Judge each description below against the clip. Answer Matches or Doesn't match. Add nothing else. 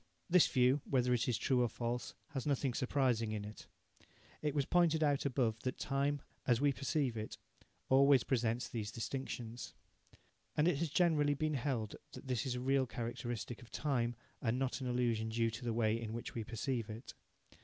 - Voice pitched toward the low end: Matches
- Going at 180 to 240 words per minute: Matches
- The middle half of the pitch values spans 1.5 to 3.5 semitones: Matches